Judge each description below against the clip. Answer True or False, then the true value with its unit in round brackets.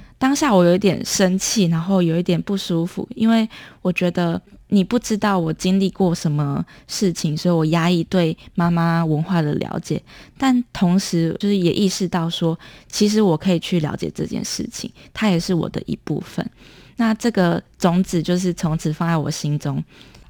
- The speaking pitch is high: False (180 Hz)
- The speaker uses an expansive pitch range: False (2.8 semitones)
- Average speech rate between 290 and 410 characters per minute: False (265 characters per minute)